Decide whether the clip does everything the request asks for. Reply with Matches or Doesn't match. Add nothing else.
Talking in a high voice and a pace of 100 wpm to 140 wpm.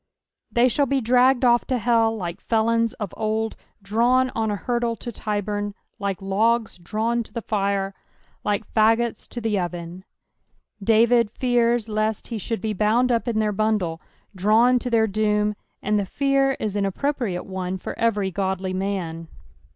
Doesn't match